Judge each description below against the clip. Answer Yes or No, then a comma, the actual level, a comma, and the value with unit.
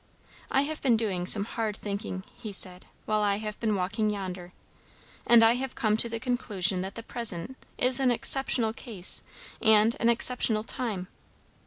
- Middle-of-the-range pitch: No, high, 220 Hz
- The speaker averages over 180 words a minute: No, average, 170 wpm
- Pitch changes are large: No, average, 3.1 semitones